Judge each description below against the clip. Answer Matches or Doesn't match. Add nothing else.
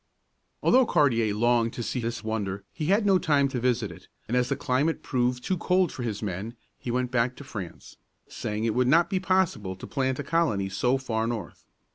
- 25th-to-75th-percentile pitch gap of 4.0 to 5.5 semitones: Matches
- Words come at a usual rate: Doesn't match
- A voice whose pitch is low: Matches